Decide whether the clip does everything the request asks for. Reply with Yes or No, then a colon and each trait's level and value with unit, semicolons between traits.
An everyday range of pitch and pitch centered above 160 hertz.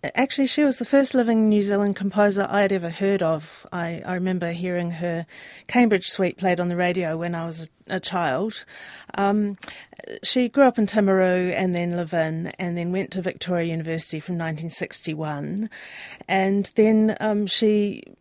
Yes: average, 3.5 semitones; high, 190 Hz